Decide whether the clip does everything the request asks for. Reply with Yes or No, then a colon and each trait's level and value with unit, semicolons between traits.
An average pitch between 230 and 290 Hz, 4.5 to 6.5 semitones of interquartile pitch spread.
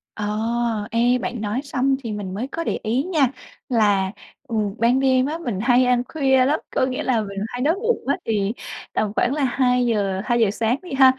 No: high, 245 Hz; average, 3.7 semitones